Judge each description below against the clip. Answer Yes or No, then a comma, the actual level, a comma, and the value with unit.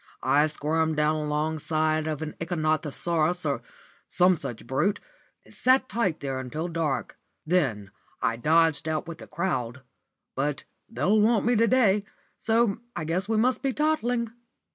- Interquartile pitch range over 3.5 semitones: Yes, wide, 5.6 semitones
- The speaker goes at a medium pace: Yes, average, 150 wpm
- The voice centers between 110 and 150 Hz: No, medium, 160 Hz